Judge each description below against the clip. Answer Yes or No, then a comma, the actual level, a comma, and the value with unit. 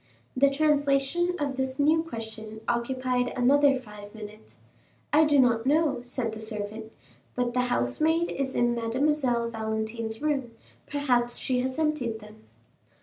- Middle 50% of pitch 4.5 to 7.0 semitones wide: No, average, 4.1 semitones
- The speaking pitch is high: Yes, very high, 250 Hz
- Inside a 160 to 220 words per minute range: No, average, 140 wpm